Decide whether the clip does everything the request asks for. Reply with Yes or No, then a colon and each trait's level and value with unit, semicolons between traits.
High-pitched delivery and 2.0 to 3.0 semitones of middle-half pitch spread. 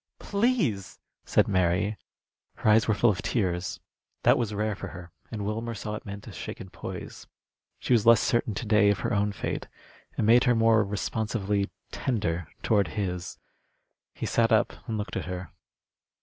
No: low, 105 Hz; narrow, 2.6 semitones